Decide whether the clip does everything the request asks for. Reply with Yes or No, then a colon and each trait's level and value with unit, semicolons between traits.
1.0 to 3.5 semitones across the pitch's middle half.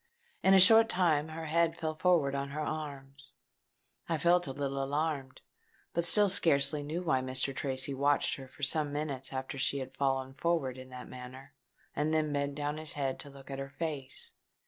Yes: average, 2.8 semitones